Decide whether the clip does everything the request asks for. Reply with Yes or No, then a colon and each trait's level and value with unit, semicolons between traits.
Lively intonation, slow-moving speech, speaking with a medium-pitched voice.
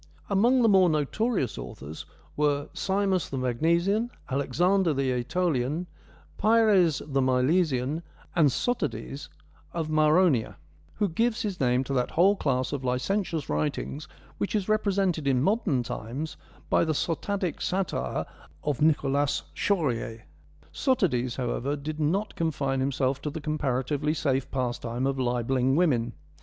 Yes: wide, 5.9 semitones; slow, 130 wpm; medium, 150 Hz